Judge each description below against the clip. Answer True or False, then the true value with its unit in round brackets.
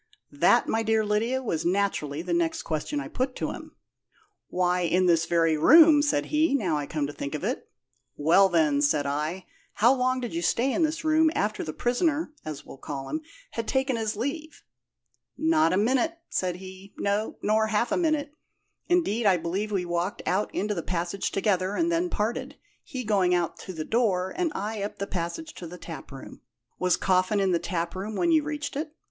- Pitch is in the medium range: False (205 Hz)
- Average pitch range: False (7.3 semitones)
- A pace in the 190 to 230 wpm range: True (200 wpm)